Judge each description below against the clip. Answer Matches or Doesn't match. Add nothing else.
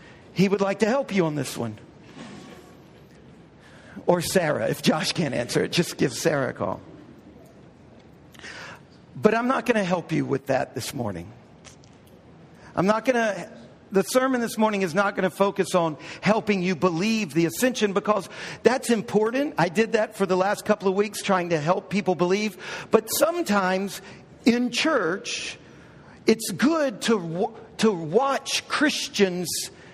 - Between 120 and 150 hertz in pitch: Doesn't match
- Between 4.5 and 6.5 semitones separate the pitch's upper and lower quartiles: Doesn't match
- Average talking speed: Matches